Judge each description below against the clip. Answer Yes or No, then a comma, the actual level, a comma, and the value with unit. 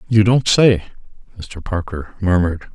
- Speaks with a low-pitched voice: Yes, very low, 95 Hz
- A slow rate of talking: Yes, slow, 130 wpm